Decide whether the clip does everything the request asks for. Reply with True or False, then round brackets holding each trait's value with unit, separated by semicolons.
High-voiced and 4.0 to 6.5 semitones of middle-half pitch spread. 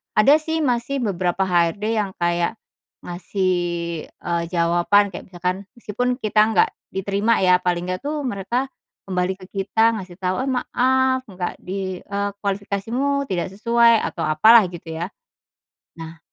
True (195 Hz; 4.6 semitones)